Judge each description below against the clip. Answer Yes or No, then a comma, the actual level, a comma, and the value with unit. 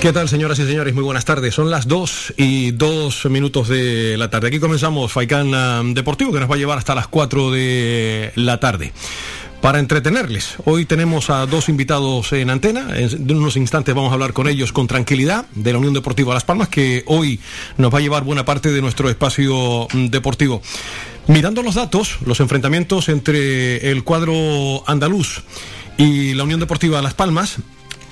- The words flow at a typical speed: Yes, average, 180 wpm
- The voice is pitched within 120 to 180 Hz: Yes, medium, 140 Hz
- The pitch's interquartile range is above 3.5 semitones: No, average, 3.2 semitones